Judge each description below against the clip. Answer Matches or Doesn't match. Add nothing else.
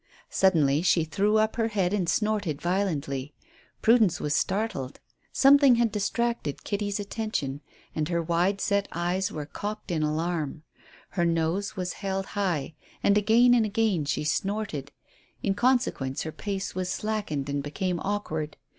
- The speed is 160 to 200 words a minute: Doesn't match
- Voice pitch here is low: Doesn't match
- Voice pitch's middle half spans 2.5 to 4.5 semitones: Doesn't match